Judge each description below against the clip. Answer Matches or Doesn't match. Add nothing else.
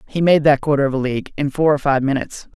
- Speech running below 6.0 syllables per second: Doesn't match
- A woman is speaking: Doesn't match